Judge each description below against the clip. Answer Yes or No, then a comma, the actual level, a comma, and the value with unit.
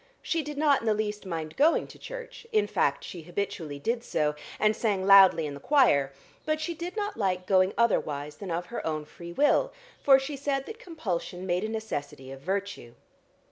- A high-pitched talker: Yes, high, 200 Hz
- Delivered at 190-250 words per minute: Yes, average, 200 wpm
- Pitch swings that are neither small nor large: No, wide, 8.8 semitones